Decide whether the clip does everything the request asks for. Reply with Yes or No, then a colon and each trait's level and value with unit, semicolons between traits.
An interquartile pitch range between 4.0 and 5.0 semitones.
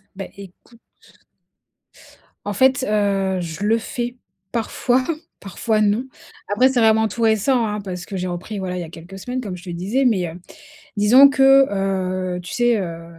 Yes: average, 4.5 semitones